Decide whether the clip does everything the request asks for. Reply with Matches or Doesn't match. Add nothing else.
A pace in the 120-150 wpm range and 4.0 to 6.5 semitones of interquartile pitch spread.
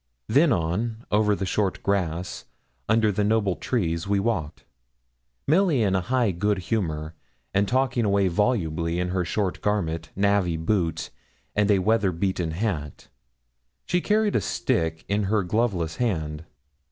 Matches